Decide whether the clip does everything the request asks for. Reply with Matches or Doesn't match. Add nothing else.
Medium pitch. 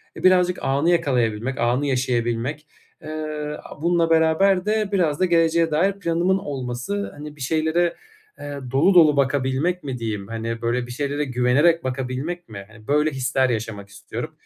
Matches